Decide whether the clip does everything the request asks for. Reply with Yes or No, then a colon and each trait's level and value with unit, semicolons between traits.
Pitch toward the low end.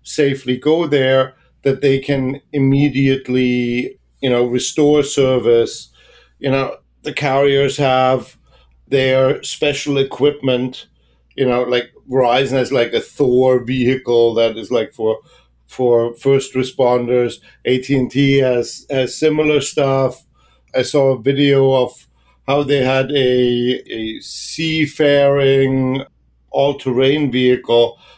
Yes: low, 130 Hz